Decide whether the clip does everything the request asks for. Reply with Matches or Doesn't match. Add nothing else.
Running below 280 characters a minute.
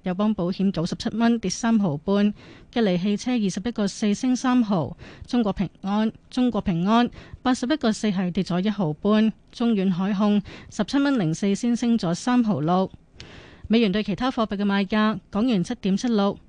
Matches